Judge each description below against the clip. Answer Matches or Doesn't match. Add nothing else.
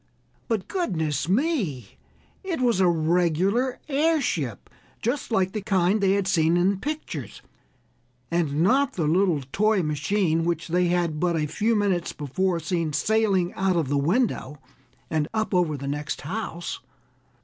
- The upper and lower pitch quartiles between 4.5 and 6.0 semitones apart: Matches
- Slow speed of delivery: Doesn't match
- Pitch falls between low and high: Matches